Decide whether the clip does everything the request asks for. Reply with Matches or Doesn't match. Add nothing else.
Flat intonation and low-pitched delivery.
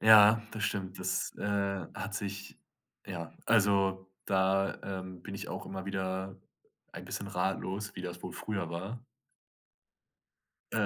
Matches